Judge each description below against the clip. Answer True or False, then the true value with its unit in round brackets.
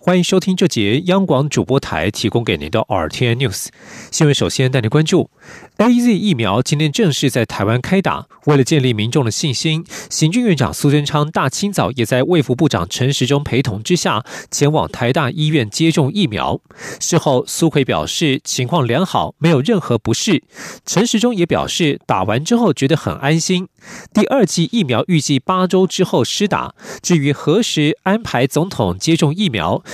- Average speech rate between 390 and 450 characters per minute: False (285 characters per minute)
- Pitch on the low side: False (150 Hz)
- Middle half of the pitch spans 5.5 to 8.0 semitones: True (6.1 semitones)